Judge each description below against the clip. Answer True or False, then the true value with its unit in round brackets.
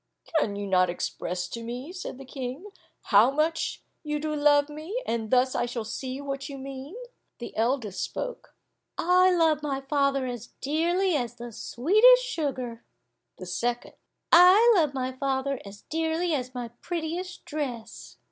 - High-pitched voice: True (275 Hz)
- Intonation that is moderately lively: True (4.9 semitones)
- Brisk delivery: False (155 wpm)